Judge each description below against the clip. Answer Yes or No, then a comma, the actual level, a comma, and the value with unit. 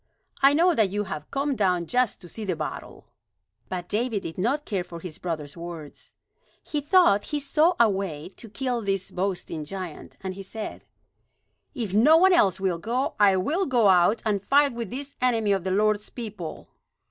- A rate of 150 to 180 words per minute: No, average, 190 wpm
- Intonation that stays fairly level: No, wide, 5.5 semitones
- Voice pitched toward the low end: No, high, 205 Hz